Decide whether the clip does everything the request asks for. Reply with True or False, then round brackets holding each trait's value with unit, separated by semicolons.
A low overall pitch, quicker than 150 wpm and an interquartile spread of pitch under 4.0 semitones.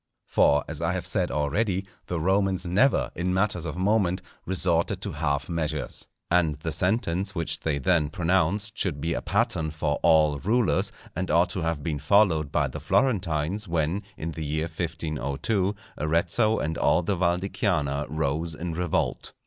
True (85 Hz; 170 wpm; 3.5 semitones)